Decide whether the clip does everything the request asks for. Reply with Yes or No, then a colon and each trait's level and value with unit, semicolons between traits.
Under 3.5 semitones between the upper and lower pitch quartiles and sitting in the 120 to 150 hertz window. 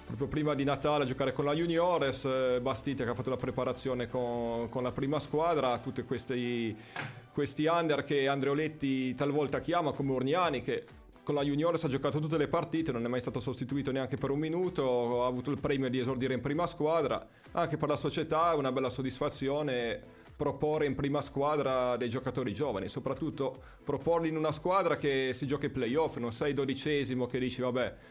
Yes: narrow, 2.6 semitones; medium, 140 Hz